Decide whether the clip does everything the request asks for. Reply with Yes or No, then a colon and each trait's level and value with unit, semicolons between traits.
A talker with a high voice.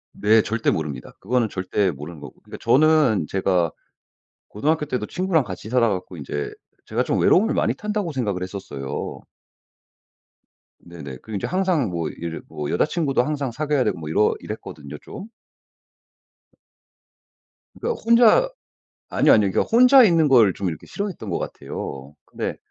No: low, 110 Hz